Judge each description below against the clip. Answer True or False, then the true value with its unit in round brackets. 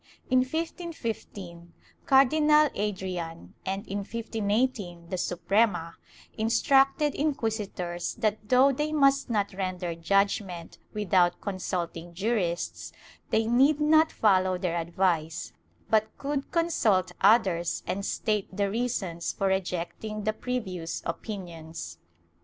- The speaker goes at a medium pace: False (105 wpm)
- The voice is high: True (200 Hz)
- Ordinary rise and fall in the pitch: False (5.7 semitones)